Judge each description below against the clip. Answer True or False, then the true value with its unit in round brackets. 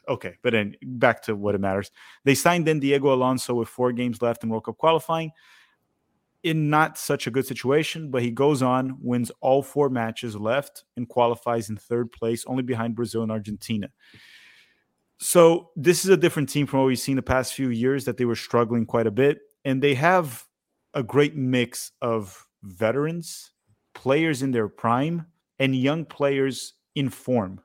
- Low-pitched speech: True (130 Hz)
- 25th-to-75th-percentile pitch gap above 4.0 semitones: False (3.7 semitones)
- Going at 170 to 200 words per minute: True (180 wpm)